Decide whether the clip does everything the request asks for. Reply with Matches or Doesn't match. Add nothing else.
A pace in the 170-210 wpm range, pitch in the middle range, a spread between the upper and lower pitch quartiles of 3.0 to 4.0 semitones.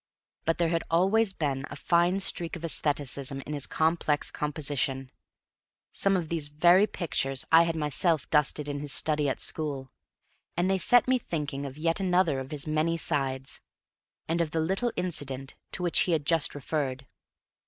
Matches